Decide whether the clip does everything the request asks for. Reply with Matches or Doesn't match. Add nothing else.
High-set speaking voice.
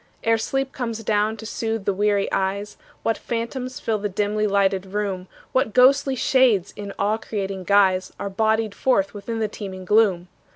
Matches